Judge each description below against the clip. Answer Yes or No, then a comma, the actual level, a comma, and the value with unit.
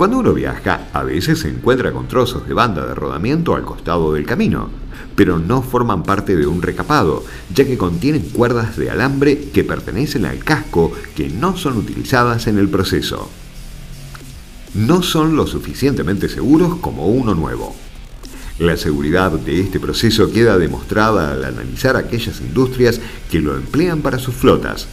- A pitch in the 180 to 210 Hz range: No, low, 105 Hz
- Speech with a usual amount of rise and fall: No, wide, 8.1 semitones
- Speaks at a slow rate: No, average, 160 wpm